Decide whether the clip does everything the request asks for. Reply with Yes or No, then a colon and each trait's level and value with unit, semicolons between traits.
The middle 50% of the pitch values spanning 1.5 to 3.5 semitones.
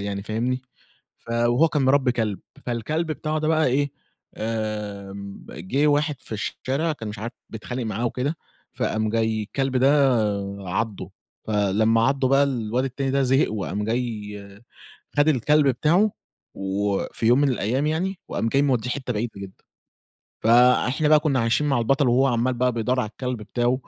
No: average, 4.1 semitones